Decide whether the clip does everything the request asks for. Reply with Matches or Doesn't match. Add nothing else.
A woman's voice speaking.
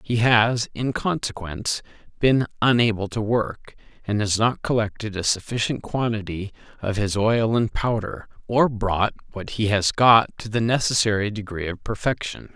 Doesn't match